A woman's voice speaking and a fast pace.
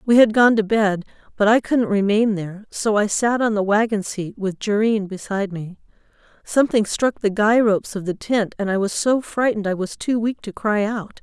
Yes: female; fast, 220 wpm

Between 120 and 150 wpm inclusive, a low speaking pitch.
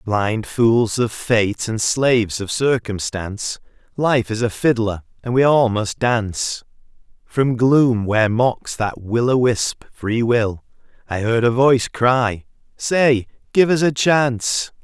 Yes: average, 140 wpm; low, 115 Hz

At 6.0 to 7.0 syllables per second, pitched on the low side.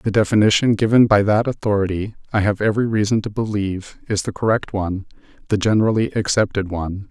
Yes: 6.3 syllables/s; low, 105 Hz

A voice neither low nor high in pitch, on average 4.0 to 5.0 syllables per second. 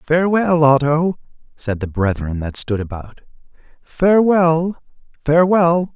Yes: medium, 150 Hz; 4.2 syllables/s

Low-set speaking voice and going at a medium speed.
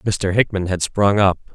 Yes: very low, 95 Hz; average, 195 wpm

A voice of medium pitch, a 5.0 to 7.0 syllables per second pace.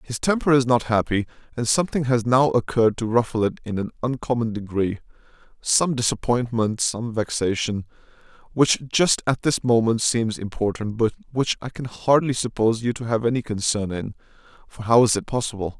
No: low, 115 Hz; 5.4 syllables/s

